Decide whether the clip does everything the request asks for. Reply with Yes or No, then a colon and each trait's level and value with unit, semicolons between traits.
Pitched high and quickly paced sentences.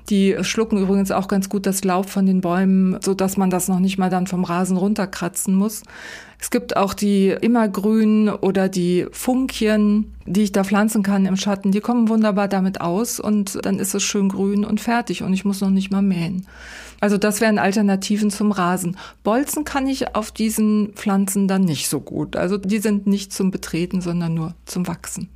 Yes: high, 200 Hz; fast, 200 wpm